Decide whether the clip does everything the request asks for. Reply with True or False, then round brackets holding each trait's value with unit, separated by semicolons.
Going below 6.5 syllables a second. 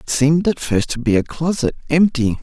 True (5.4 syllables/s)